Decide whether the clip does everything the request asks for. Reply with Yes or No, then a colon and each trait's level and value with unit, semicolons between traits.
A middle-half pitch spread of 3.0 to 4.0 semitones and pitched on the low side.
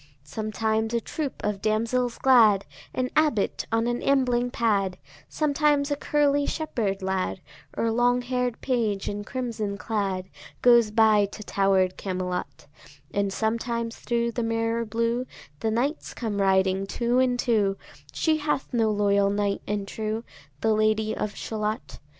No: average, 3.3 semitones; high, 225 Hz